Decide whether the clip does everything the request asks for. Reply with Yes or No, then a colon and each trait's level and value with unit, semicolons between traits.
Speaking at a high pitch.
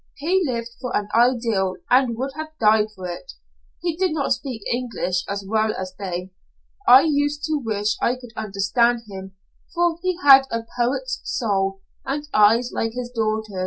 Yes: high, 235 Hz